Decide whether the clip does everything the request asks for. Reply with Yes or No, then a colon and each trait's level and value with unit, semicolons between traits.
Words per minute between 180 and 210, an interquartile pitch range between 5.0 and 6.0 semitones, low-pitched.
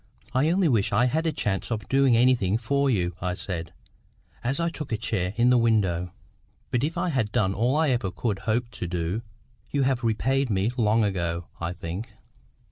Yes: average, 200 wpm; wide, 5.5 semitones; low, 115 Hz